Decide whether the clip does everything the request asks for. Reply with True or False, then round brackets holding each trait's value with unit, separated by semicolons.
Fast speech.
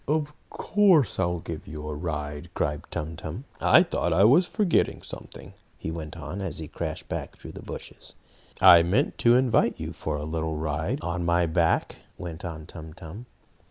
False (185 wpm)